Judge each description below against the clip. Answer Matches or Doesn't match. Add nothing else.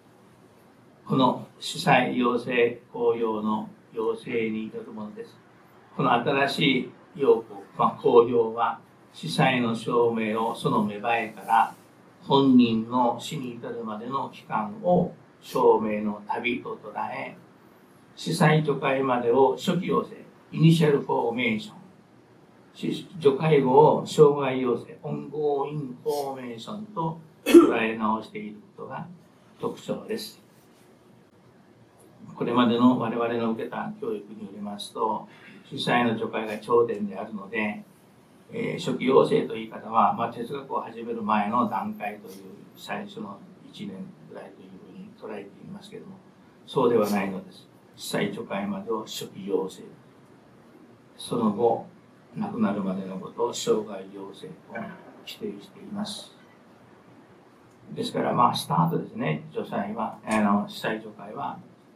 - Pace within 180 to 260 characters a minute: Matches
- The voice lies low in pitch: Matches